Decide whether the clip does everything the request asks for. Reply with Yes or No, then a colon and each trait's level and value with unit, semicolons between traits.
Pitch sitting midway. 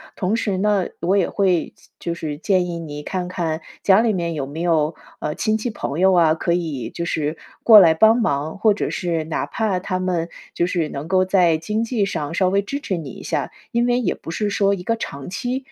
Yes: medium, 180 Hz